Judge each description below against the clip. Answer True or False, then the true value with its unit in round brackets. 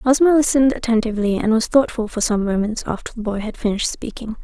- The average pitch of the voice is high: True (230 Hz)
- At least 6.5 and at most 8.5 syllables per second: True (6.6 syllables/s)